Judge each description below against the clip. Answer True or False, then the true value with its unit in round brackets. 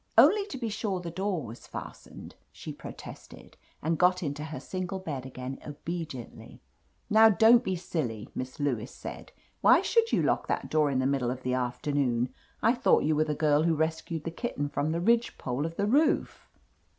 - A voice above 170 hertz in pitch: False (155 Hz)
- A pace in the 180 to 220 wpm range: True (190 wpm)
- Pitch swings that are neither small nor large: False (5.8 semitones)